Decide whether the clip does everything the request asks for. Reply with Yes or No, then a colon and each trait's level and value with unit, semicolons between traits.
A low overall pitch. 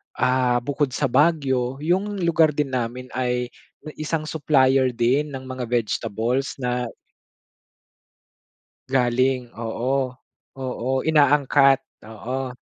Yes: low, 130 Hz